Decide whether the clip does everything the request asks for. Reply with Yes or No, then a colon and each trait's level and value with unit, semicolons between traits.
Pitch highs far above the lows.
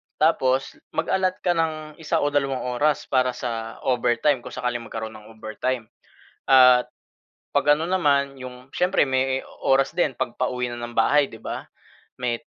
No: average, 3.3 semitones